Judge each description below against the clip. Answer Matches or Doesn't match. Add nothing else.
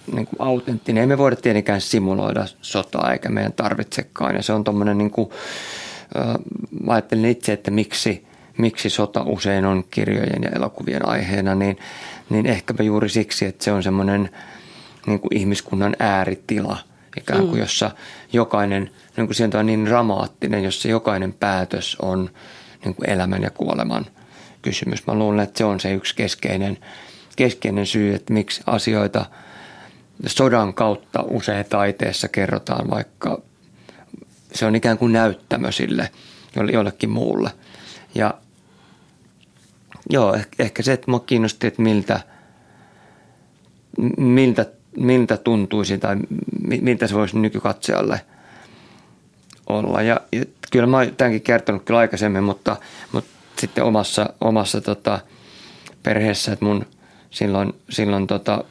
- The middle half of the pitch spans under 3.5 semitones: Matches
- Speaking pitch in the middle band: Doesn't match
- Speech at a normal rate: Matches